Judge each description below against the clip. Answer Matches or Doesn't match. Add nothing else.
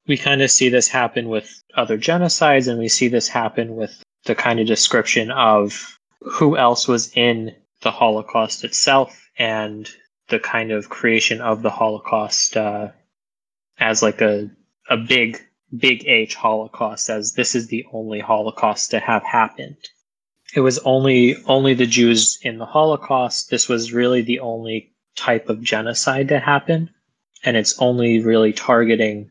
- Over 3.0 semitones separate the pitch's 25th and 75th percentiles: Doesn't match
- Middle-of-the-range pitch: Doesn't match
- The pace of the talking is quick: Doesn't match